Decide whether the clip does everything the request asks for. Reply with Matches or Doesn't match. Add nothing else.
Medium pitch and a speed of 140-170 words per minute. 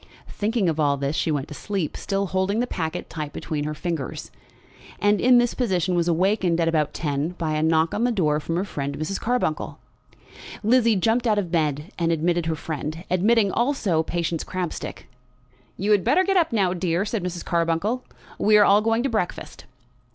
Doesn't match